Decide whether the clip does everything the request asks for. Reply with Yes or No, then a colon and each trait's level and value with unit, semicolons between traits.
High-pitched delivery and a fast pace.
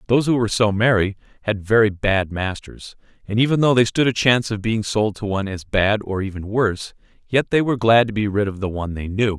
No: low, 105 Hz; fast, 245 wpm